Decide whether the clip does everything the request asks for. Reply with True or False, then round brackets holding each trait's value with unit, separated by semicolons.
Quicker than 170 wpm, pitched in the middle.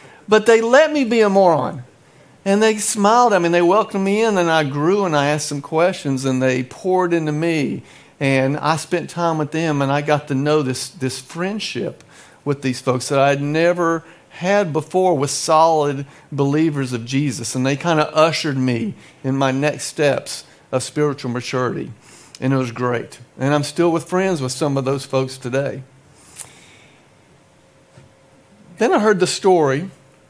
True (180 wpm; 150 Hz)